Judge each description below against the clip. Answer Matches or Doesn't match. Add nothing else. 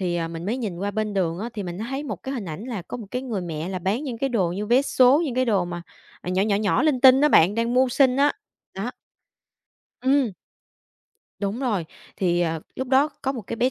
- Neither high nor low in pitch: Doesn't match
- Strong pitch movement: Matches